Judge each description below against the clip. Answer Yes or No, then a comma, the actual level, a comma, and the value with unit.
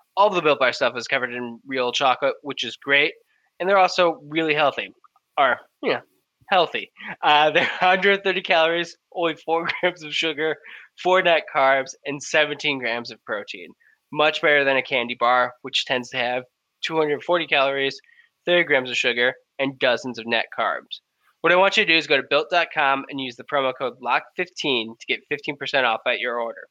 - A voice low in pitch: No, medium, 150 Hz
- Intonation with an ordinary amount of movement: Yes, average, 4.5 semitones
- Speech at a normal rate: Yes, average, 185 wpm